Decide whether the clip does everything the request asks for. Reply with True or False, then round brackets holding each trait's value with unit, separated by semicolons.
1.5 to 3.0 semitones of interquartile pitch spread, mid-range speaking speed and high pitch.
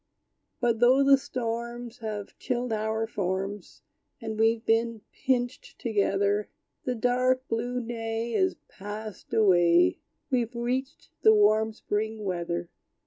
False (2.6 semitones; 120 wpm; 225 Hz)